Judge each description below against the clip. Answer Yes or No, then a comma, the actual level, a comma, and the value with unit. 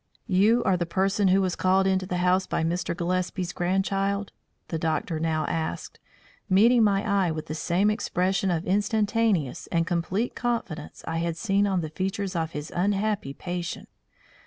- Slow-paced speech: No, average, 165 wpm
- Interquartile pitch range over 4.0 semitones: No, average, 2.9 semitones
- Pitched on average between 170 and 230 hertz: Yes, medium, 185 Hz